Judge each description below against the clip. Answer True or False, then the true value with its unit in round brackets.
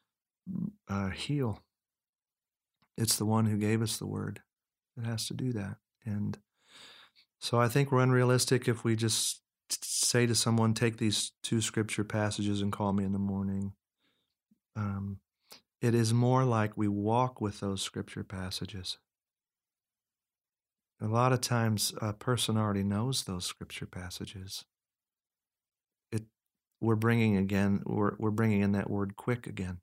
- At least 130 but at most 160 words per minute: True (145 wpm)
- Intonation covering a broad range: False (2.7 semitones)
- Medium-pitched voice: False (110 Hz)